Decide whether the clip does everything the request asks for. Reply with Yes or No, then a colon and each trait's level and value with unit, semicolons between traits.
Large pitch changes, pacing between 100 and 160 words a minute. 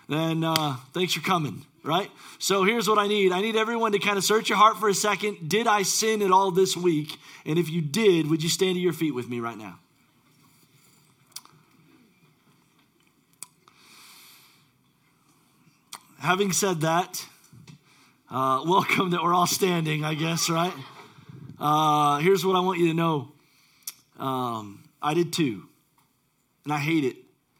No: average, 4.4 semitones; average, 155 wpm